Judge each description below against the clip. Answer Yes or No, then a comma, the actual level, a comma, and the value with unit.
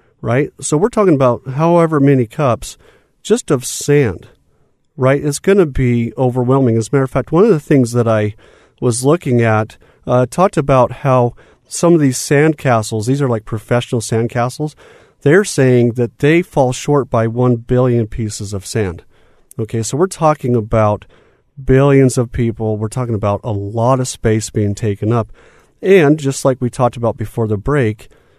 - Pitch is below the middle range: Yes, low, 125 Hz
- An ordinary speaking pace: Yes, average, 175 wpm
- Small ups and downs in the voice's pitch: No, average, 3.9 semitones